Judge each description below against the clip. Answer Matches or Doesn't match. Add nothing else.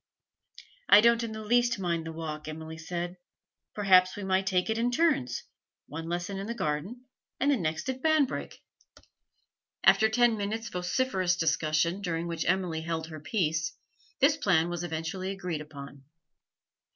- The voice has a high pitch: Doesn't match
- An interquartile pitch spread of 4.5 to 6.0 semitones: Matches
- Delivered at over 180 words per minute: Doesn't match